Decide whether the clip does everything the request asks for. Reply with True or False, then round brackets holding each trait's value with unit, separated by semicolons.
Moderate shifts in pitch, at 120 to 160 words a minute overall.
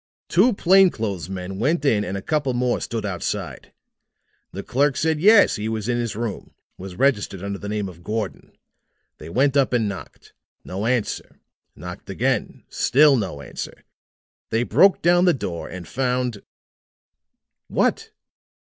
False (6.0 semitones; 155 wpm)